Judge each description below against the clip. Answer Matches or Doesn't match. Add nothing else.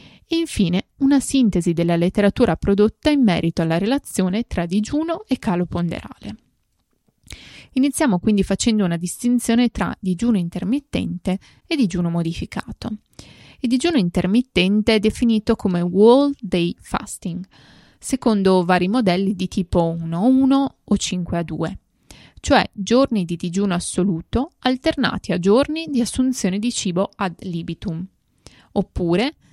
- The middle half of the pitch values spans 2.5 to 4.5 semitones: Doesn't match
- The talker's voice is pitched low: Doesn't match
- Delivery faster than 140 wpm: Doesn't match